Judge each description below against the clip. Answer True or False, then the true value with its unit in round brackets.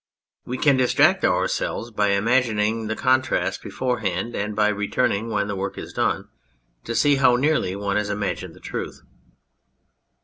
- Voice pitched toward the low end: True (110 Hz)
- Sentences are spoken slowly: False (160 wpm)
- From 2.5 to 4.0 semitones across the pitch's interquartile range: True (3.6 semitones)